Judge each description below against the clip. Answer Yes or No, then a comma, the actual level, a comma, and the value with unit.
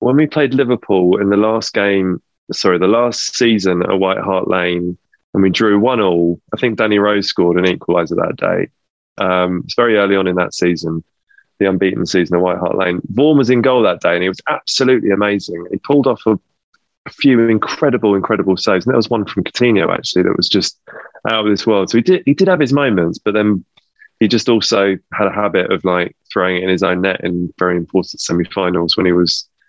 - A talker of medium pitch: No, low, 100 Hz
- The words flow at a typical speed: No, fast, 225 wpm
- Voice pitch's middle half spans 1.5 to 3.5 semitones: No, average, 4.0 semitones